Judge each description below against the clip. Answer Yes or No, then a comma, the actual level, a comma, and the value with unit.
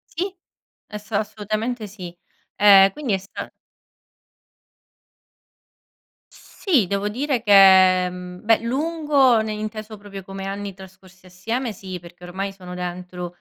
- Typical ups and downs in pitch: Yes, average, 3.1 semitones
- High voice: Yes, high, 200 Hz